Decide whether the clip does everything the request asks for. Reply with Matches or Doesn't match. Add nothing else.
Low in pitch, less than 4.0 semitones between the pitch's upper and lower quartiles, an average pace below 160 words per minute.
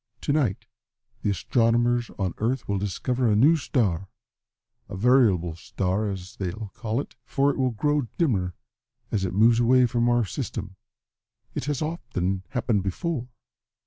Doesn't match